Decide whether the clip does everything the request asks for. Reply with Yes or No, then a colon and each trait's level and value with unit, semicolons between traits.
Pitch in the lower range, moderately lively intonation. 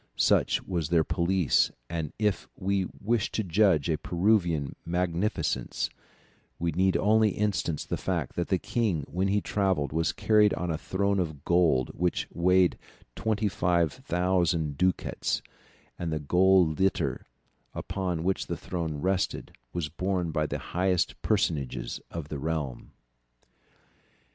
Yes: very low, 90 Hz; average, 3.0 semitones